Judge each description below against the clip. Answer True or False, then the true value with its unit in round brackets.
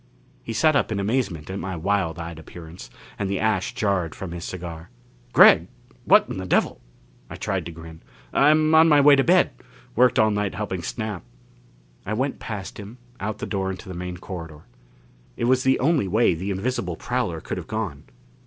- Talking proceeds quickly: False (195 wpm)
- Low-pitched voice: True (100 Hz)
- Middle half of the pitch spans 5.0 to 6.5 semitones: True (5.3 semitones)